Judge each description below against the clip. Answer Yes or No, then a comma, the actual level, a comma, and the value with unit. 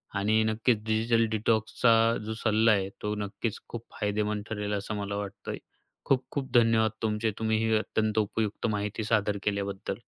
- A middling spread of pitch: No, narrow, 1.3 semitones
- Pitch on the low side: Yes, low, 110 Hz